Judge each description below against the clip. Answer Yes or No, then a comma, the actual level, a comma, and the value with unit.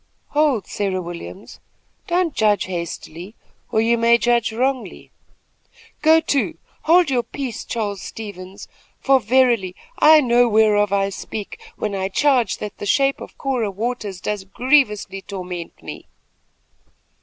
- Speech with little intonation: No, average, 4.8 semitones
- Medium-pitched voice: No, high, 220 Hz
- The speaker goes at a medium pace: No, slow, 130 wpm